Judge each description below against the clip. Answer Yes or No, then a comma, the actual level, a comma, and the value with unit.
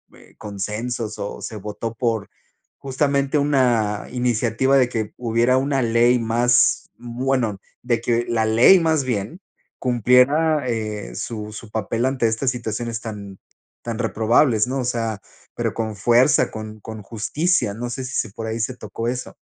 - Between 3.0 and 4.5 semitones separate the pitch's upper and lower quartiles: No, narrow, 2.6 semitones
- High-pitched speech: No, low, 115 Hz